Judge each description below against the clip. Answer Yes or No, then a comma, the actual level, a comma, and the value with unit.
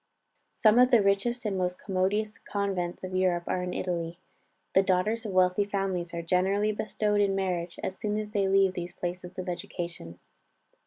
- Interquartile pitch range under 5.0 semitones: Yes, narrow, 2.4 semitones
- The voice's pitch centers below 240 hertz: Yes, high, 190 Hz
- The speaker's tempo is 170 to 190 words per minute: Yes, average, 175 wpm